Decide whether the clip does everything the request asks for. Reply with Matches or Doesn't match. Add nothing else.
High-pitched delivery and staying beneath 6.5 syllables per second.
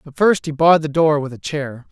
Doesn't match